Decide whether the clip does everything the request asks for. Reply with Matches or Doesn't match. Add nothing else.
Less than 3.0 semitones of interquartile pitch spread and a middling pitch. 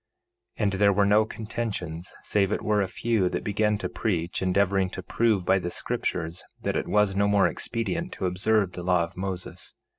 Doesn't match